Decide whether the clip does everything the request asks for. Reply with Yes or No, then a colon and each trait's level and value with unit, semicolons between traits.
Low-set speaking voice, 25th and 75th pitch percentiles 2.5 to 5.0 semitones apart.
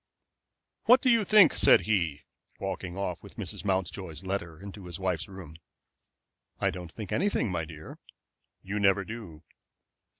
Yes: very low, 95 Hz; average, 3.4 semitones